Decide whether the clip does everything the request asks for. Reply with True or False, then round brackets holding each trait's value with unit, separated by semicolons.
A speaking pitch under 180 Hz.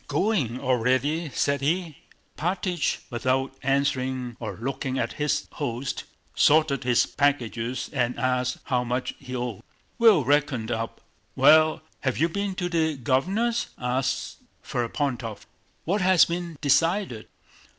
True (135 Hz)